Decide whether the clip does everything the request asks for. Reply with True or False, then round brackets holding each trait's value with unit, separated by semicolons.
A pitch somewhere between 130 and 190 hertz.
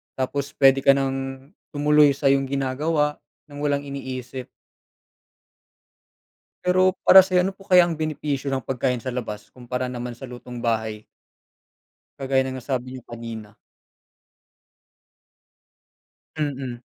True (135 Hz)